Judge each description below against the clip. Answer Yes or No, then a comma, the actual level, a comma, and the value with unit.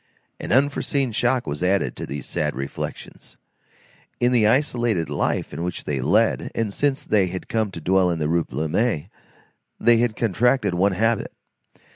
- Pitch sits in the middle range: No, low, 105 Hz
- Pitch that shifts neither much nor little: No, wide, 5.8 semitones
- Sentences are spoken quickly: No, average, 160 wpm